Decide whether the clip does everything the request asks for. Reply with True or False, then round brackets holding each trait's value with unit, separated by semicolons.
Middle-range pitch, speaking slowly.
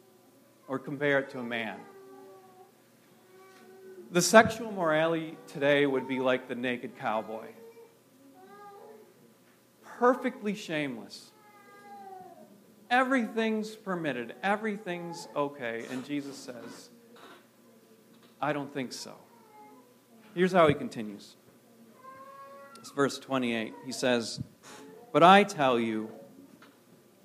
True (175 Hz; 90 wpm)